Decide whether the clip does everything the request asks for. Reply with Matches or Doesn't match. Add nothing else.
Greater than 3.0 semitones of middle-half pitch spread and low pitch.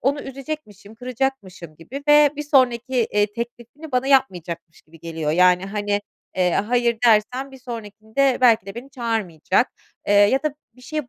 Doesn't match